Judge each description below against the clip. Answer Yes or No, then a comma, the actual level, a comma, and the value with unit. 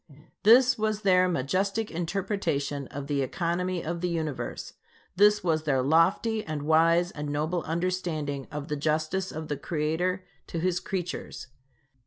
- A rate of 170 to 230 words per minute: No, average, 145 wpm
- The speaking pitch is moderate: Yes, medium, 170 Hz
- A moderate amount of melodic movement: Yes, average, 3.4 semitones